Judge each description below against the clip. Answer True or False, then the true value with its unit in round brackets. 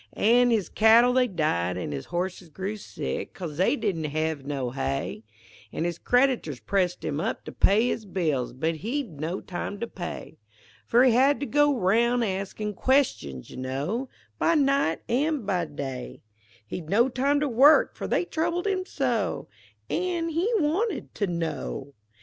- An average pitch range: False (8.9 semitones)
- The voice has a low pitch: False (200 Hz)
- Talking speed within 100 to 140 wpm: False (165 wpm)